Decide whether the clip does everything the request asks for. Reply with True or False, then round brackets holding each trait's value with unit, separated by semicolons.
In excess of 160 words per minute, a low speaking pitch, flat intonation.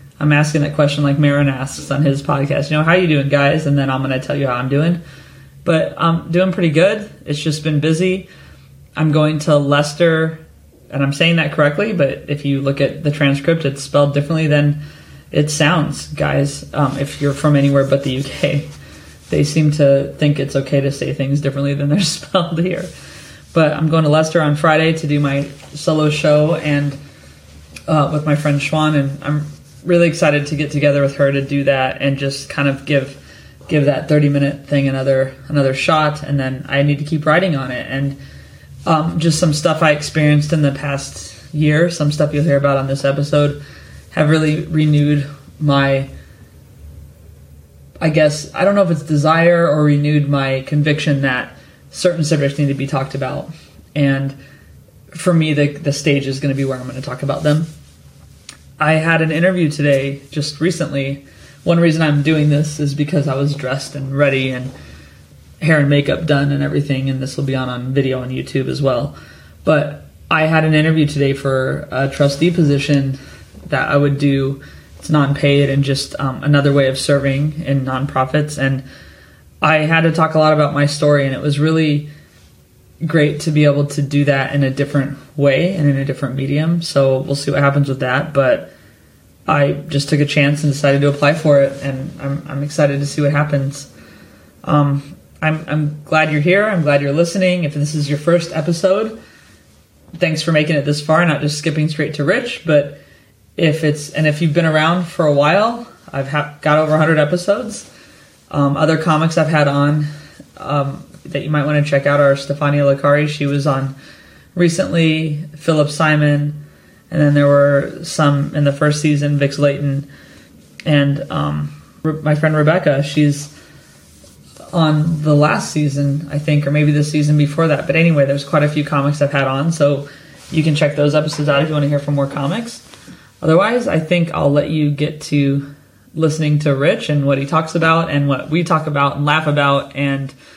False (195 wpm; 145 Hz; 1.9 semitones)